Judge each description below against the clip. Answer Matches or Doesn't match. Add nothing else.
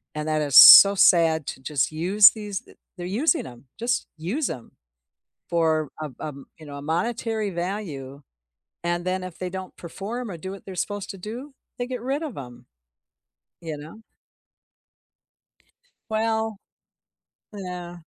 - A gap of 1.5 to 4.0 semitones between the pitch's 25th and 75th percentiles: Doesn't match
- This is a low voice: Doesn't match